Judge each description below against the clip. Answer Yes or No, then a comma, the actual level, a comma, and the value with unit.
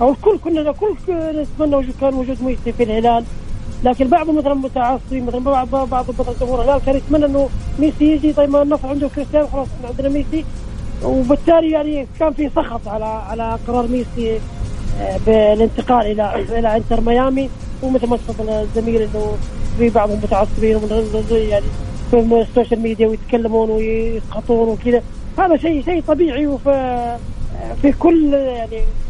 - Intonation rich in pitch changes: No, average, 4.2 semitones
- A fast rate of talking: No, average, 155 wpm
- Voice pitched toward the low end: No, very high, 250 Hz